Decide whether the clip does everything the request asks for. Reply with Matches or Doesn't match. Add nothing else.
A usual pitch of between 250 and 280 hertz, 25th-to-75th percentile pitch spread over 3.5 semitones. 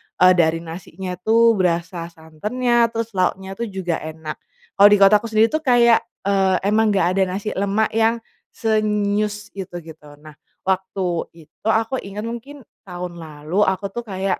Doesn't match